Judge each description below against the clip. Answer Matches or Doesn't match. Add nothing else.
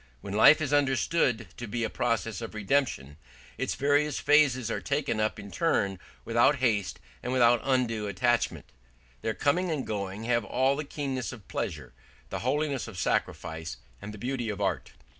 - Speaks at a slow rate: Doesn't match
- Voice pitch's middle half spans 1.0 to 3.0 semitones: Doesn't match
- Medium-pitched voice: Doesn't match